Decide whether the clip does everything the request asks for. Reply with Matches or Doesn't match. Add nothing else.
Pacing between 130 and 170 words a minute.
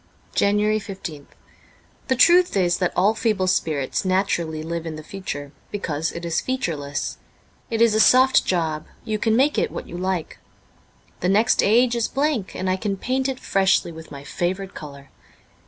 Doesn't match